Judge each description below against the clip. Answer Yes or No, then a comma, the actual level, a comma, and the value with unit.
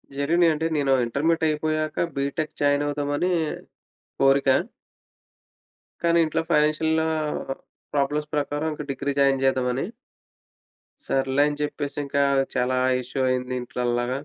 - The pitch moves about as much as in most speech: No, narrow, 2.3 semitones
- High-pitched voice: No, medium, 145 Hz